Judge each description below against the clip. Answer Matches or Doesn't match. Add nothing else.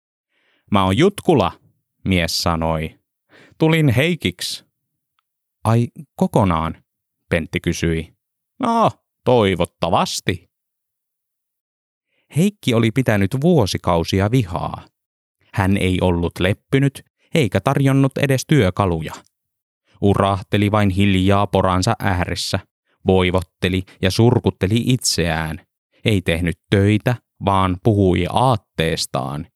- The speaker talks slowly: Matches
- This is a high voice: Doesn't match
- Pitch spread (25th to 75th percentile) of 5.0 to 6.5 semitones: Matches